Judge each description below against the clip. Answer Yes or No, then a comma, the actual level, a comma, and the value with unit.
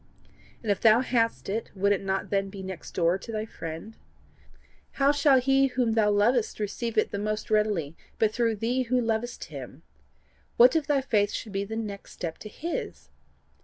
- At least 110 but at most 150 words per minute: No, average, 190 wpm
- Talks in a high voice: Yes, high, 220 Hz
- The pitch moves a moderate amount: Yes, average, 3.3 semitones